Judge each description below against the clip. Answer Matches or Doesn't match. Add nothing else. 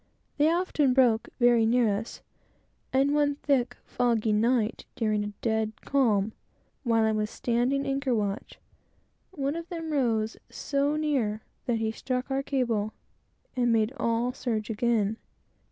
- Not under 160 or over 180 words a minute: Doesn't match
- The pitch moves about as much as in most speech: Matches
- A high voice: Matches